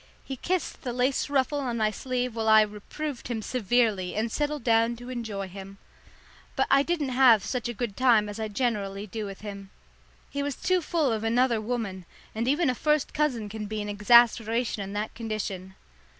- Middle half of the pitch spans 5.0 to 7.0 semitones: No, average, 3.7 semitones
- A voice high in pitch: Yes, high, 230 Hz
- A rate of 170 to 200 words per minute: Yes, average, 195 wpm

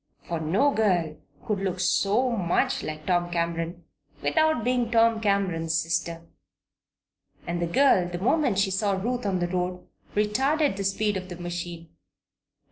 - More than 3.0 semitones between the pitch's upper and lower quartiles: Yes, average, 4.2 semitones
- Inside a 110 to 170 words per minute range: Yes, average, 150 wpm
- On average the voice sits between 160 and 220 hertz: Yes, high, 190 Hz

